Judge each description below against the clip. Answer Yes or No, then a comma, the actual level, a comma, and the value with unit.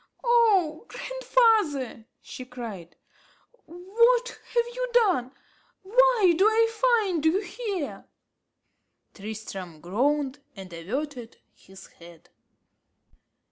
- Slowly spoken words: Yes, slow, 90 wpm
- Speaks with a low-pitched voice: No, very high, 335 Hz